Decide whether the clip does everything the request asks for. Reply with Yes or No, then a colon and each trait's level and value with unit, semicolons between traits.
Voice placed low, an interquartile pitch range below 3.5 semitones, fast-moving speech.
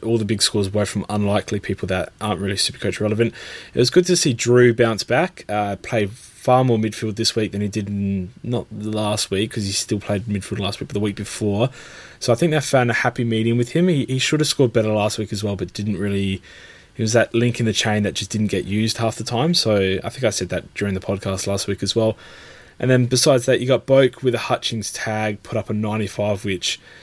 Yes: low, 110 Hz; average, 2.9 semitones; fast, 255 wpm